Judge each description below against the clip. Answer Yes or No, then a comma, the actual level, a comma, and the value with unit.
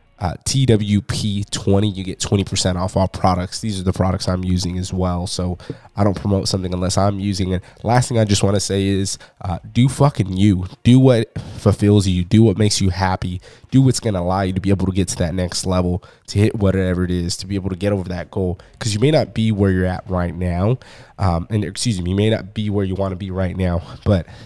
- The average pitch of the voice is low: Yes, low, 100 Hz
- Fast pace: Yes, fast, 250 wpm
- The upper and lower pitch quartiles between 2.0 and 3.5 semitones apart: Yes, average, 2.9 semitones